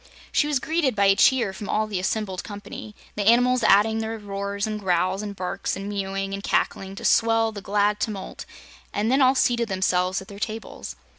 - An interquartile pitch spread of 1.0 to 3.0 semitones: Yes, narrow, 2.4 semitones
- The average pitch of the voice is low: No, high, 205 Hz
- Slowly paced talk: No, average, 200 wpm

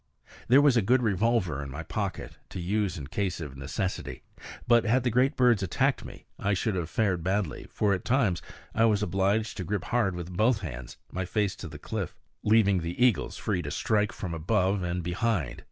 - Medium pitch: No, low, 100 Hz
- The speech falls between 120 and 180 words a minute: No, average, 200 wpm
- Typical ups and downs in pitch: Yes, average, 4.2 semitones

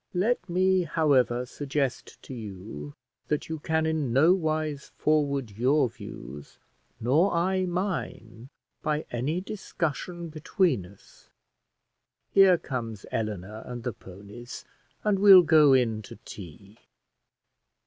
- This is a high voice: No, medium, 140 Hz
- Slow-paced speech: Yes, slow, 120 wpm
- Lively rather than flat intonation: Yes, wide, 7.0 semitones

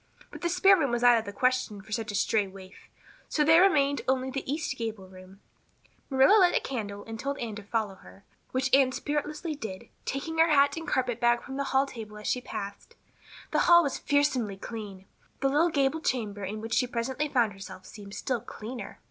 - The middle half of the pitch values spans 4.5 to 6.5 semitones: Yes, average, 5.1 semitones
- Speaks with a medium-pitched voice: No, very high, 250 Hz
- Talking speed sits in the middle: No, fast, 210 wpm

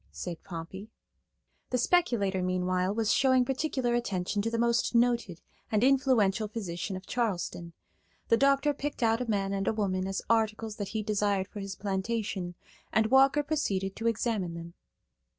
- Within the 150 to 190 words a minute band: Yes, average, 160 wpm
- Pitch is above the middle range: Yes, high, 215 Hz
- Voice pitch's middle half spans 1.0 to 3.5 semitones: No, average, 3.9 semitones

